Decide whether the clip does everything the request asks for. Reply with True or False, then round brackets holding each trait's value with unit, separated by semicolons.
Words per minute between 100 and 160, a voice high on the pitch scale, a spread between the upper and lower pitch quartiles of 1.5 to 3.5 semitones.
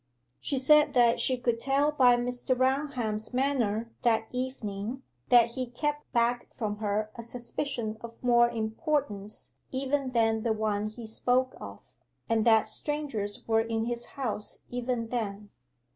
True (145 wpm; 240 Hz; 2.8 semitones)